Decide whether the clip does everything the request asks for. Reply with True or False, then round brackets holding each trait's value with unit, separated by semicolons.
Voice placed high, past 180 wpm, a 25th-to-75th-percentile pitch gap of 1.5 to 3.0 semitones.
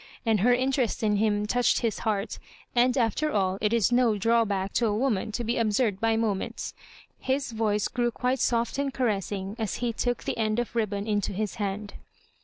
True (225 Hz; 200 wpm; 2.7 semitones)